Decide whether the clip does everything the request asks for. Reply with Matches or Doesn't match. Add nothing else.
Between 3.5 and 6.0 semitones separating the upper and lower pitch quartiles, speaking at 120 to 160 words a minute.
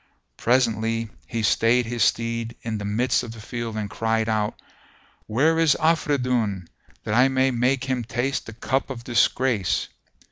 Doesn't match